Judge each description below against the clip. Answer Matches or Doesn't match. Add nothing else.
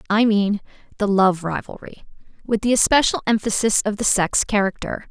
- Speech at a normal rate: Matches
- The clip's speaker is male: Doesn't match